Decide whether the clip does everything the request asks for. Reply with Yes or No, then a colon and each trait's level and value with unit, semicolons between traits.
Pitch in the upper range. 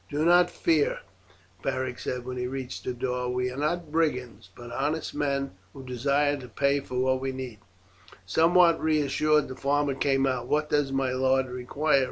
No: low, 135 Hz